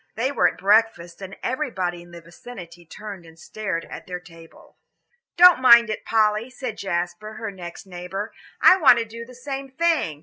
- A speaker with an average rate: Yes, average, 180 wpm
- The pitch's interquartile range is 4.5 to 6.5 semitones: Yes, wide, 5.5 semitones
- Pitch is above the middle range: Yes, high, 210 Hz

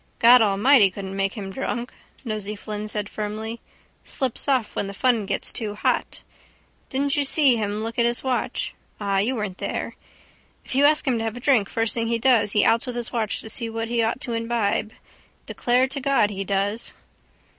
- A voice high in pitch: Yes, high, 225 Hz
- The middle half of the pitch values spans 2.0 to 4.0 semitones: Yes, average, 3.1 semitones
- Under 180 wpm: No, average, 200 wpm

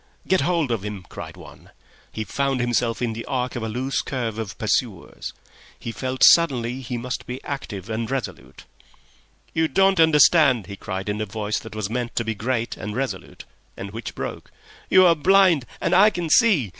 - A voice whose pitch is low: Yes, low, 125 Hz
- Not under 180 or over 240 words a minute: Yes, average, 190 wpm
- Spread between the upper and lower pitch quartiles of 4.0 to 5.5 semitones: Yes, average, 4.5 semitones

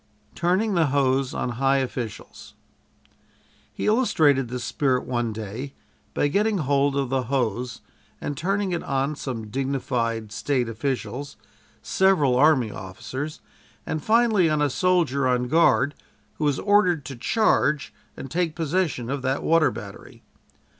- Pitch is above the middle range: No, medium, 140 Hz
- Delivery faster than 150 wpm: No, average, 140 wpm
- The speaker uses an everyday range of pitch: Yes, average, 4.4 semitones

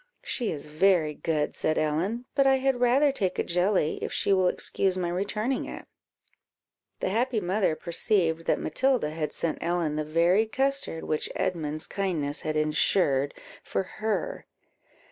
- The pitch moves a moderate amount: No, wide, 5.9 semitones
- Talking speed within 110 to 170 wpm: Yes, average, 155 wpm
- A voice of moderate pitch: Yes, medium, 180 Hz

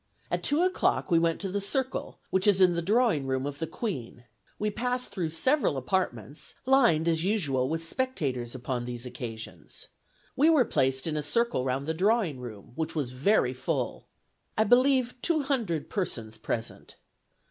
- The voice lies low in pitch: No, medium, 165 Hz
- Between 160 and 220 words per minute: Yes, average, 170 wpm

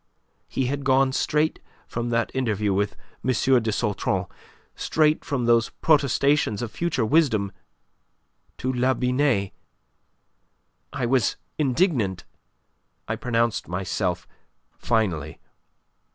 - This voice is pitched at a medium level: No, low, 120 Hz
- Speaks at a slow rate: Yes, slow, 105 wpm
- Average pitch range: Yes, average, 4.5 semitones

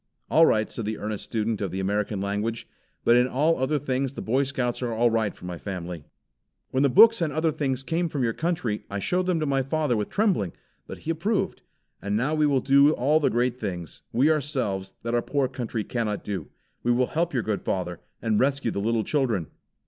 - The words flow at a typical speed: No, fast, 220 wpm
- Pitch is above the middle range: No, low, 125 Hz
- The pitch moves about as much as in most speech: No, wide, 5.7 semitones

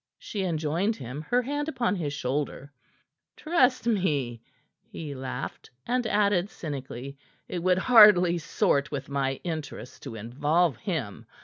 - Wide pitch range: Yes, wide, 6.8 semitones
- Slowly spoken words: Yes, slow, 130 wpm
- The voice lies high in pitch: No, medium, 160 Hz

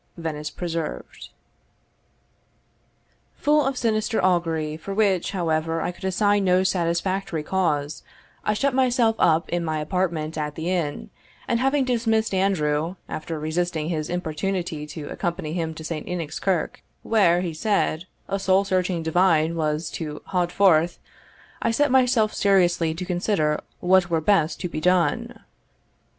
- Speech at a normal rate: Yes, average, 145 wpm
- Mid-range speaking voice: Yes, medium, 175 Hz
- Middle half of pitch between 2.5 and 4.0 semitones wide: Yes, average, 3.6 semitones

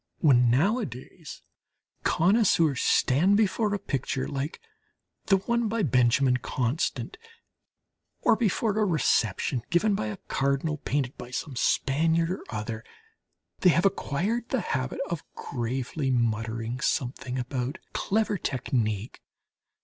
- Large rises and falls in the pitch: Yes, wide, 7.3 semitones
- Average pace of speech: No, slow, 120 wpm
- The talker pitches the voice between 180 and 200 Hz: No, medium, 140 Hz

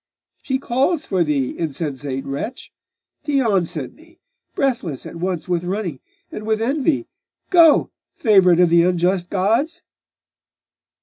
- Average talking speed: No, slow, 125 wpm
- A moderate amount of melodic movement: No, wide, 7.6 semitones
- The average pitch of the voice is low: No, high, 190 Hz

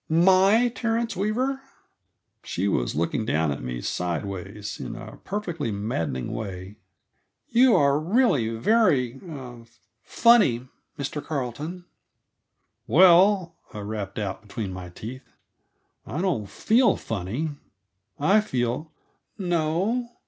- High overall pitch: No, medium, 140 Hz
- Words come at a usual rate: No, slow, 115 wpm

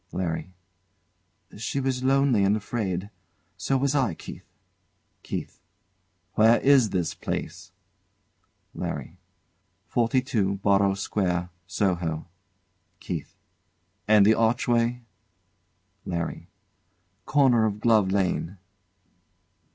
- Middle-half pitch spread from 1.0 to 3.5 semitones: No, average, 4.4 semitones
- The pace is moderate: No, slow, 90 wpm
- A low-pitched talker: Yes, low, 105 Hz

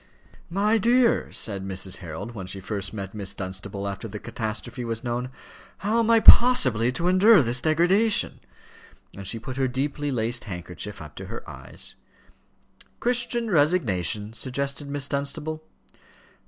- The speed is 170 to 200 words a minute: No, average, 145 wpm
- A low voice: Yes, low, 125 Hz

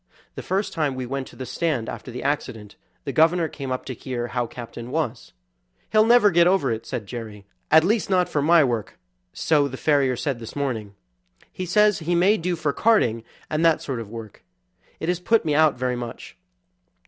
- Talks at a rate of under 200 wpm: No, fast, 205 wpm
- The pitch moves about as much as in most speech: No, wide, 5.9 semitones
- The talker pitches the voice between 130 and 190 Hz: Yes, medium, 140 Hz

